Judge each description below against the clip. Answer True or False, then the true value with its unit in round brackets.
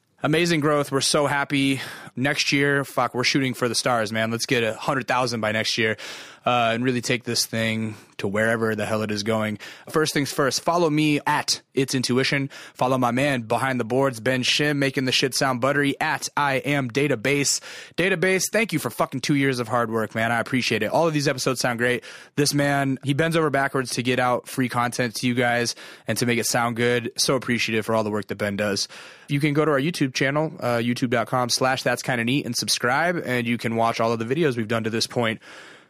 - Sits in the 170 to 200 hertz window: False (125 Hz)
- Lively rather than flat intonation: False (3.3 semitones)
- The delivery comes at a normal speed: False (230 wpm)